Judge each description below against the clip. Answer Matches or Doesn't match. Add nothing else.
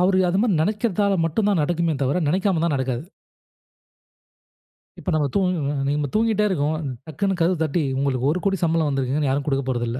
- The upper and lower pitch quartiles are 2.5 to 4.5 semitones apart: Doesn't match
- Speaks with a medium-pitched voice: Matches